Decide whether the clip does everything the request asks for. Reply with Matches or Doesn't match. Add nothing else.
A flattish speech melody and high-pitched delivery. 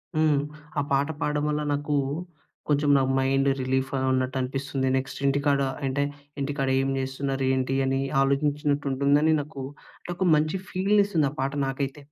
Doesn't match